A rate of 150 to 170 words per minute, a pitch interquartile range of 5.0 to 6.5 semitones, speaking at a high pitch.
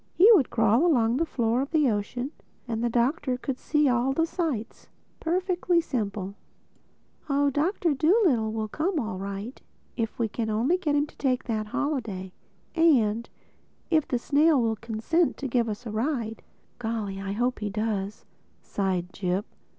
Yes: average, 160 wpm; wide, 5.4 semitones; high, 240 Hz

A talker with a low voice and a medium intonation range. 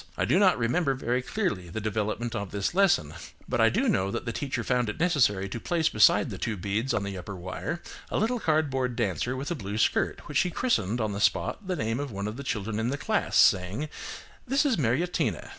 No: low, 120 Hz; wide, 7.1 semitones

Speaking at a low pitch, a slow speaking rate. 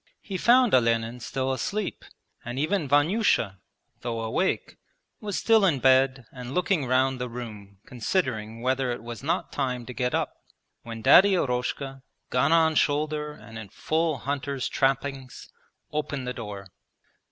No: low, 130 Hz; average, 145 wpm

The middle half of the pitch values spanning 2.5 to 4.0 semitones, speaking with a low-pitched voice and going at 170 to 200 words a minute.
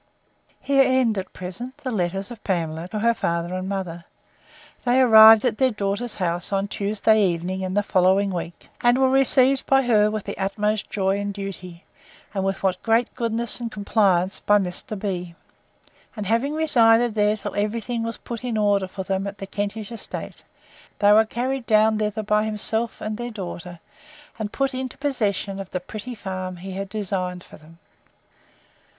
No: average, 3.3 semitones; high, 210 Hz; average, 180 wpm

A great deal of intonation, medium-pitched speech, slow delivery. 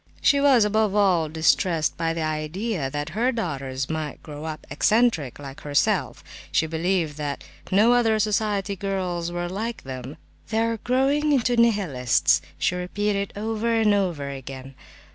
No: wide, 6.4 semitones; medium, 180 Hz; average, 150 wpm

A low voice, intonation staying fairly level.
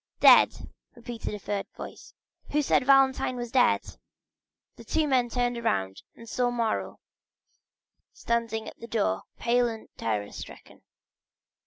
No: high, 235 Hz; narrow, 2.1 semitones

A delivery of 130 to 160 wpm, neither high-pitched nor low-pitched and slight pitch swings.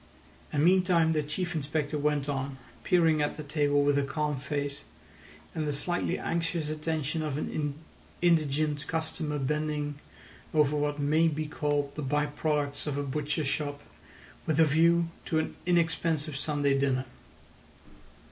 Yes: average, 145 wpm; medium, 150 Hz; narrow, 1.8 semitones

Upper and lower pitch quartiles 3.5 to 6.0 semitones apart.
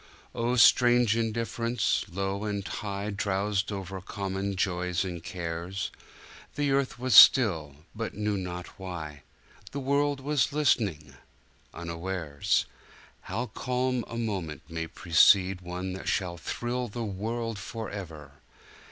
Yes: average, 4.7 semitones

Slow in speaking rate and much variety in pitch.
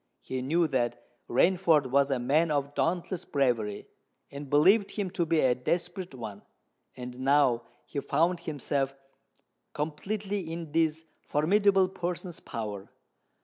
No: slow, 130 wpm; average, 4.9 semitones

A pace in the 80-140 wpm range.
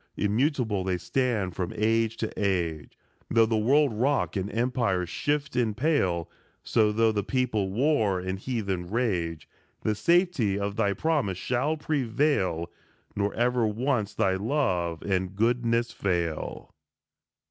Yes: slow, 135 wpm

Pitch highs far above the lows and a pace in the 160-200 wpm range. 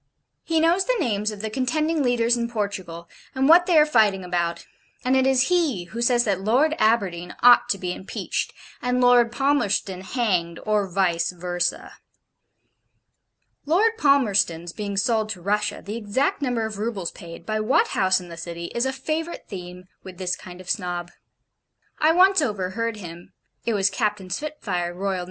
Yes: wide, 5.9 semitones; average, 170 wpm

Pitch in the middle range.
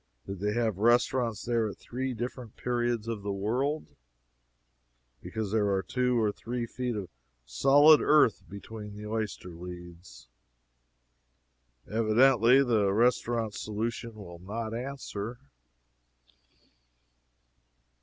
No: low, 115 Hz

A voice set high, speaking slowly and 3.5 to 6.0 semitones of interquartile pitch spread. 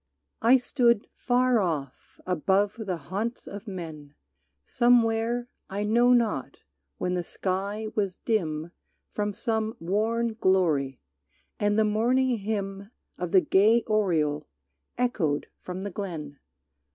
Yes: high, 205 Hz; slow, 120 wpm; average, 4.1 semitones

